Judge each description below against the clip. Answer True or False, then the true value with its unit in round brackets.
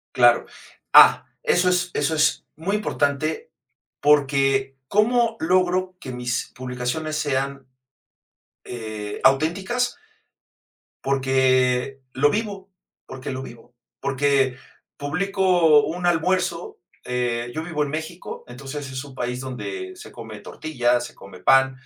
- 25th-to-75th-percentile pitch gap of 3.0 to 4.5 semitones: False (5.4 semitones)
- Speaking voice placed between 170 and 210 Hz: False (140 Hz)